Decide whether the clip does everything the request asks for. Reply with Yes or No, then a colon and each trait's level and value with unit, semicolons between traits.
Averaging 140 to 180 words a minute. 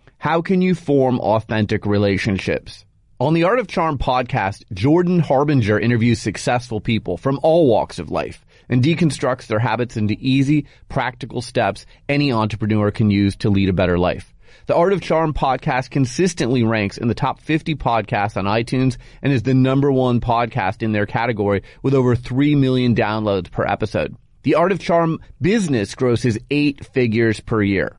Yes: average, 170 wpm